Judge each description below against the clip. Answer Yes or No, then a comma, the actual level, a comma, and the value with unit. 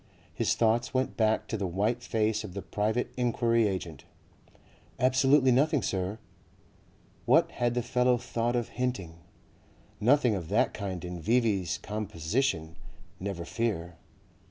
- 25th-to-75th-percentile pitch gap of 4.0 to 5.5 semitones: Yes, average, 4.5 semitones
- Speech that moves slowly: Yes, slow, 130 wpm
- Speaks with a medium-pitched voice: No, low, 110 Hz